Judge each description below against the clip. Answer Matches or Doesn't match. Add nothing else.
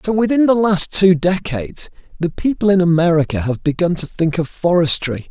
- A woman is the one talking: Doesn't match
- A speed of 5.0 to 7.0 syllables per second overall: Matches